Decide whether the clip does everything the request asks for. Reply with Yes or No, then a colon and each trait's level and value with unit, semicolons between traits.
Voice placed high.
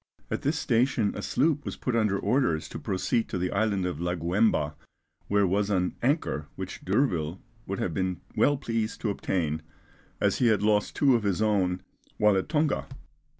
No: low, 100 Hz